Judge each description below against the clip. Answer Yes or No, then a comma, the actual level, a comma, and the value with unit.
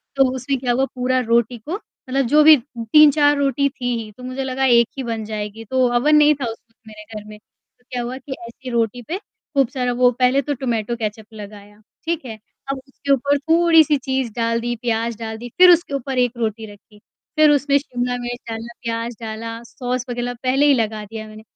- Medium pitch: No, high, 245 Hz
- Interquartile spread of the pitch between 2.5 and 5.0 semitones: Yes, average, 3.1 semitones